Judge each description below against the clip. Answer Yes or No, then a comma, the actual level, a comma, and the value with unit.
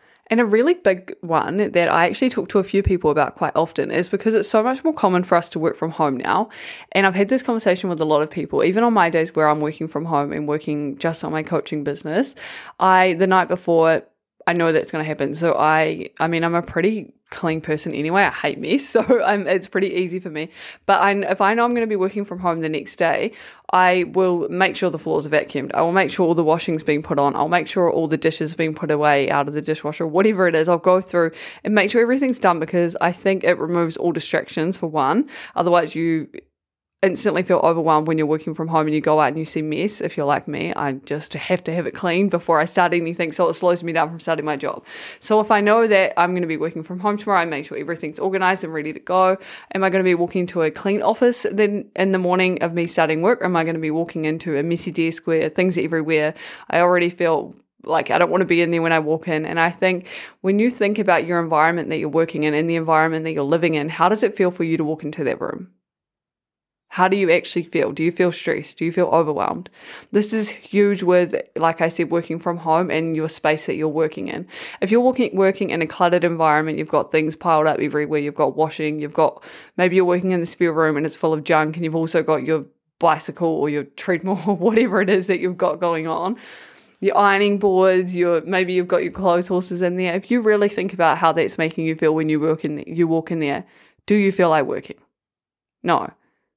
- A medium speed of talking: No, fast, 255 wpm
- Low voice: No, medium, 170 Hz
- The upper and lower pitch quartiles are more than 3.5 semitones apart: No, average, 3.0 semitones